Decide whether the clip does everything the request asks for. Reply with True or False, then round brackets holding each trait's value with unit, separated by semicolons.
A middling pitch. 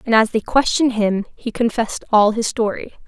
False (225 Hz)